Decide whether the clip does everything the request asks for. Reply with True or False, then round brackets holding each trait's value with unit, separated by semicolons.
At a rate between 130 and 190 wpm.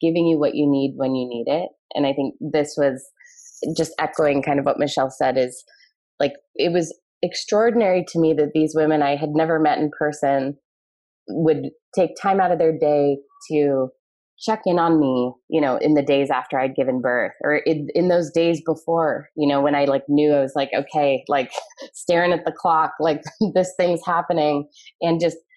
False (200 wpm)